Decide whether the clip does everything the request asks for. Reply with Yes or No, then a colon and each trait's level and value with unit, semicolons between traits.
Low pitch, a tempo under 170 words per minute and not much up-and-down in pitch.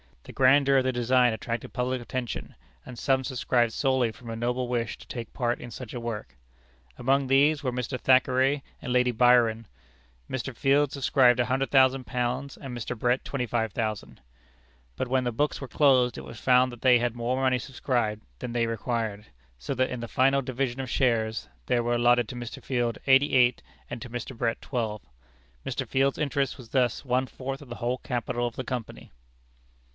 No: low, 125 Hz; average, 185 wpm; narrow, 1.8 semitones